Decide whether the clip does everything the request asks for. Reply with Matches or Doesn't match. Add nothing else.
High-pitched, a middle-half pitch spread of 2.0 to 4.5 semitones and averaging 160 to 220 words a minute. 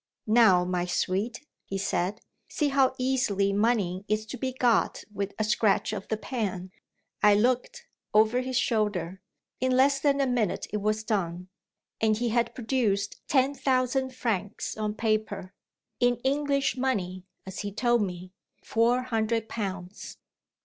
Doesn't match